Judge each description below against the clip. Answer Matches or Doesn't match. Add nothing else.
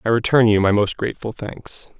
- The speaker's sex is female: Doesn't match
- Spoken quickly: Matches